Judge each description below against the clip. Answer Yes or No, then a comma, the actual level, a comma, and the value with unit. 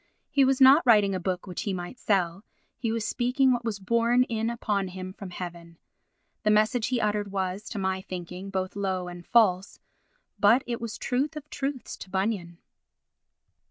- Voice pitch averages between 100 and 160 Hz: No, high, 205 Hz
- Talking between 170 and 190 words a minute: Yes, average, 180 wpm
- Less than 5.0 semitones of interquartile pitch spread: Yes, average, 4.2 semitones